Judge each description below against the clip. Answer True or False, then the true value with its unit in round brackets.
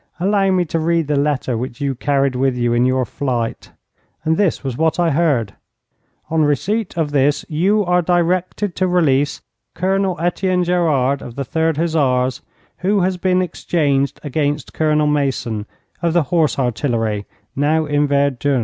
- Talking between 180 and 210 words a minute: False (160 wpm)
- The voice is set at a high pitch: False (150 Hz)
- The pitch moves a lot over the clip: False (4.5 semitones)